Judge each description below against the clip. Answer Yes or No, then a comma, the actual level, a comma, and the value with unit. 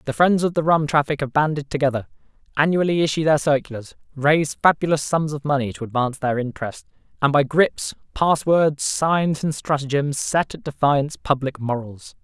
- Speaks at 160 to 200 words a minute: Yes, average, 170 wpm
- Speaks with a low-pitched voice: No, medium, 145 Hz